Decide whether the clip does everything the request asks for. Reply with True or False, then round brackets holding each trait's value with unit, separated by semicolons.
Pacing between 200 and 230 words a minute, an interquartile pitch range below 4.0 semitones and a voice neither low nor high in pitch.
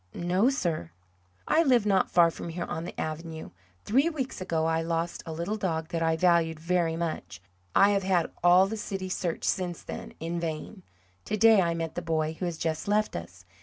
True (205 wpm; 3.0 semitones; 170 Hz)